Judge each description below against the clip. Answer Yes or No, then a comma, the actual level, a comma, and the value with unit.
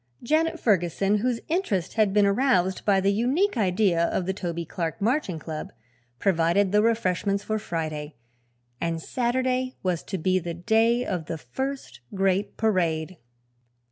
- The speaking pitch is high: Yes, high, 195 Hz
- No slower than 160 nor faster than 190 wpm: No, average, 145 wpm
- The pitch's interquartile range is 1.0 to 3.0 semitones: No, average, 5.0 semitones